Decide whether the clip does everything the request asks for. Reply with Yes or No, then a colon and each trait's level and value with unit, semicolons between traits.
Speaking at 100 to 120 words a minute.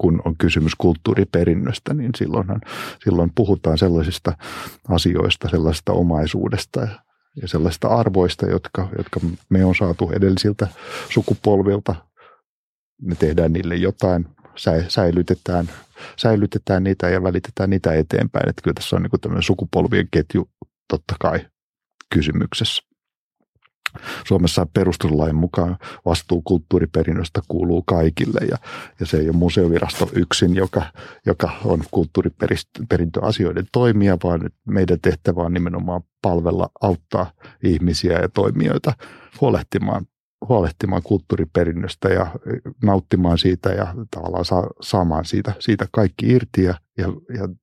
Yes: average, 115 wpm